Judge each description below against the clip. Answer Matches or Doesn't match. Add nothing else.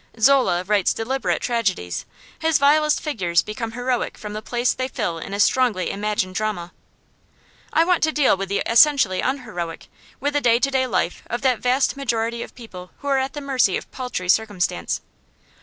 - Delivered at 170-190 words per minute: Matches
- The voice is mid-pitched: Doesn't match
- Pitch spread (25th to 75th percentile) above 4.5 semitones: Matches